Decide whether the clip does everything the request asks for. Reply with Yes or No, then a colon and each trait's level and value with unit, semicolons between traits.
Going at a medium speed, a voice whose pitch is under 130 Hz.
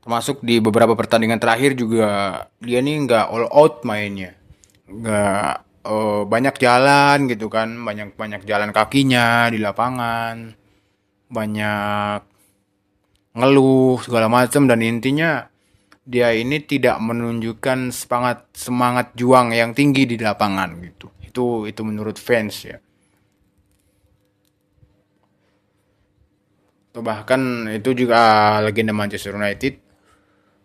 Yes: average, 105 wpm; low, 110 Hz